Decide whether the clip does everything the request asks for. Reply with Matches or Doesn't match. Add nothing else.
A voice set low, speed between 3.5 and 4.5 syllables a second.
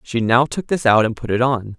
Doesn't match